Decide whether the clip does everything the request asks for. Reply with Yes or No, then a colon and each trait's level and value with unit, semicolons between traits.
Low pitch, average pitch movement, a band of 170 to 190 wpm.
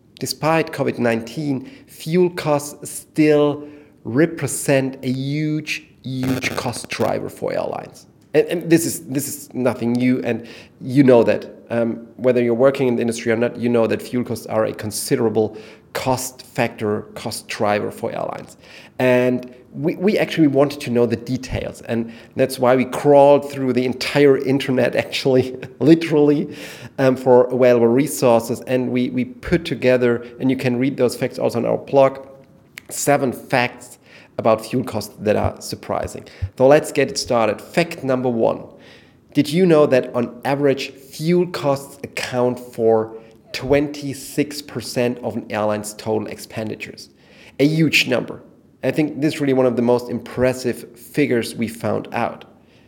No: low, 130 Hz; average, 3.0 semitones; average, 155 wpm